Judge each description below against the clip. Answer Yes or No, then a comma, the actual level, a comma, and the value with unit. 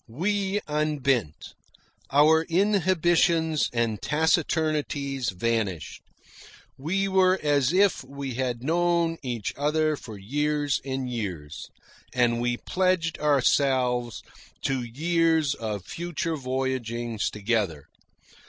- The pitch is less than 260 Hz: Yes, medium, 140 Hz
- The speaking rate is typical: No, slow, 95 wpm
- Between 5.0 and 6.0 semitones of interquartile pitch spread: Yes, wide, 5.4 semitones